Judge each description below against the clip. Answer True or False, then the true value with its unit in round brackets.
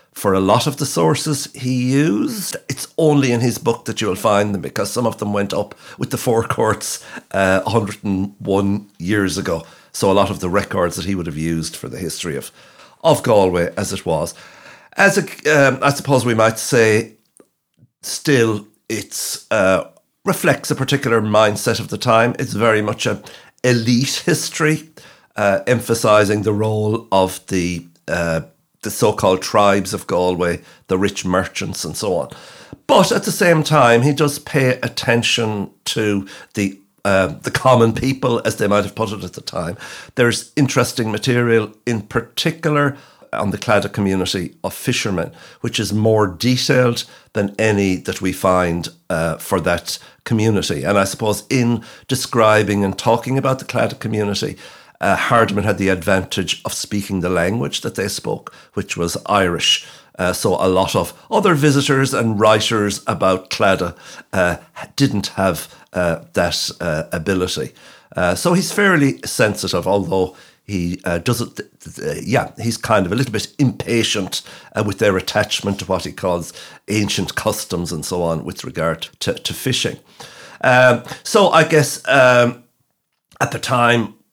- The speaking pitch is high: False (110 Hz)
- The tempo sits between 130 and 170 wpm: True (165 wpm)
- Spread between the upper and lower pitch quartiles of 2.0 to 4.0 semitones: False (4.4 semitones)